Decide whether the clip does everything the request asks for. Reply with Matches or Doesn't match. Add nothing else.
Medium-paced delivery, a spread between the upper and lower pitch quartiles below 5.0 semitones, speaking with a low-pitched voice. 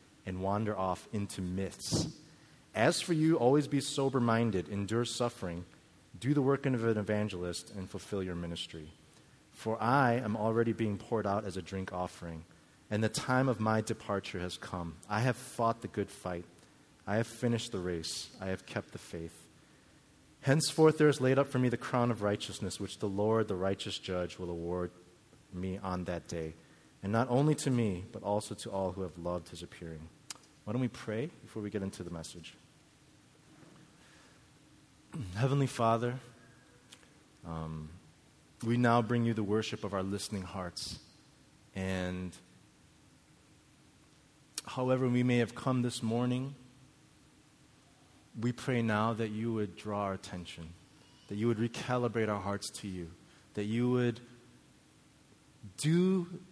Doesn't match